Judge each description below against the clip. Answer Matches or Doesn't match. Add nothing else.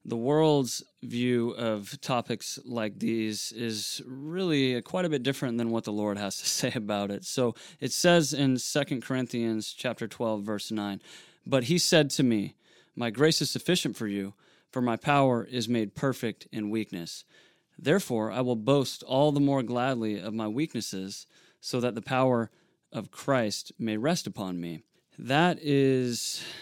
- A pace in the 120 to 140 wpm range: Doesn't match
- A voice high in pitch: Doesn't match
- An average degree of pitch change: Matches